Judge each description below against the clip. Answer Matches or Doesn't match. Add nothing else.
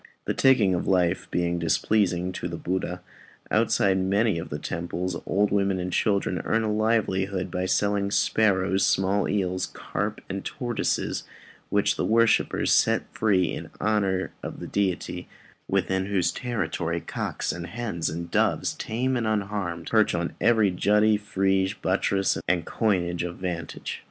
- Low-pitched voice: Matches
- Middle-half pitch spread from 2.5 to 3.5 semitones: Matches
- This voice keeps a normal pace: Matches